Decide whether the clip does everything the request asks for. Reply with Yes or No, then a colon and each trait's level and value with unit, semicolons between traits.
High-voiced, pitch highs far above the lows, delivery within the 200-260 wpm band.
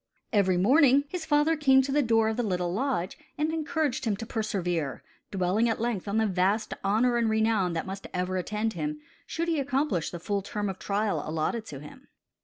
Yes: high, 215 Hz; wide, 6.0 semitones; fast, 205 wpm